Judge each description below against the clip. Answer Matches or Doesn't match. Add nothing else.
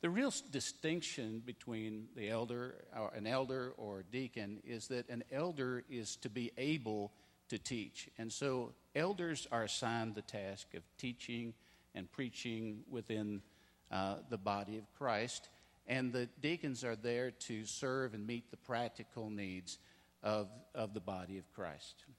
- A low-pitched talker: Matches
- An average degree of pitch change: Matches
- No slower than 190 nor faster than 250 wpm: Doesn't match